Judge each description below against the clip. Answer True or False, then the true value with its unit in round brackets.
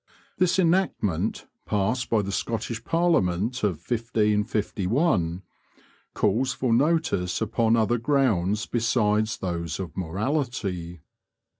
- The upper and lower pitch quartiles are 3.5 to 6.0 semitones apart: True (4.8 semitones)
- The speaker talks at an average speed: False (100 wpm)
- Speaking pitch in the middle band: False (110 Hz)